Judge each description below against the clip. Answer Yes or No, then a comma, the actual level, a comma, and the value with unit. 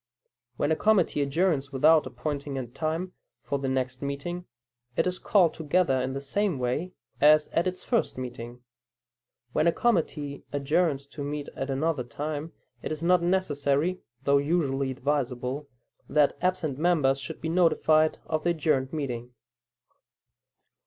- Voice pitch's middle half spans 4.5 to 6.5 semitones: No, average, 3.7 semitones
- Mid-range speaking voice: Yes, medium, 150 Hz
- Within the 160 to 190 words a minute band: No, average, 145 wpm